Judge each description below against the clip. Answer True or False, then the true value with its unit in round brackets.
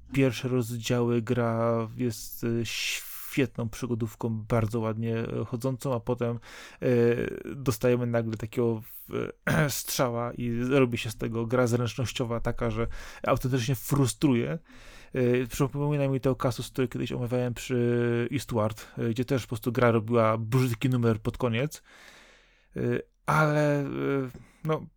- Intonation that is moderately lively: False (2.1 semitones)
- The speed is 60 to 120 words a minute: True (115 wpm)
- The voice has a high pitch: False (120 Hz)